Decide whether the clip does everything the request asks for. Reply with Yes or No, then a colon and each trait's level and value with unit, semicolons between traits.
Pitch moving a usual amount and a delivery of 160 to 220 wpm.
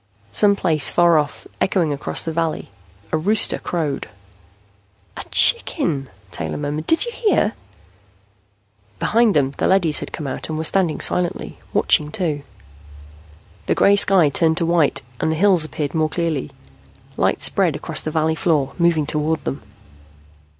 No: average, 3.2 semitones; average, 150 wpm